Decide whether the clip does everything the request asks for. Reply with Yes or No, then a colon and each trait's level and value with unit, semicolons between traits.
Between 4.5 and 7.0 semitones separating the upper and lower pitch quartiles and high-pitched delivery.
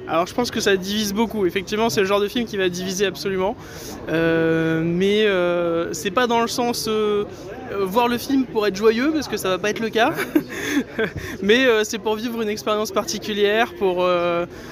No: average, 3.3 semitones; high, 210 Hz